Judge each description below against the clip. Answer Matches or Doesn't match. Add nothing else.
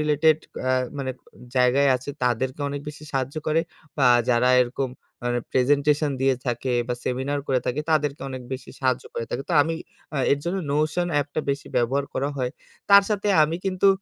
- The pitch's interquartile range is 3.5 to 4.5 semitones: Doesn't match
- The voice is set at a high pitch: Doesn't match